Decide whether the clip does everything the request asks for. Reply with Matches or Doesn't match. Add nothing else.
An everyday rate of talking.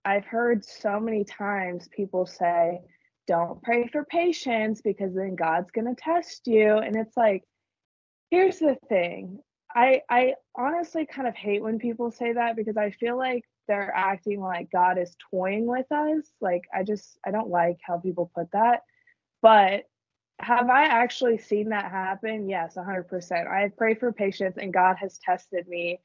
Matches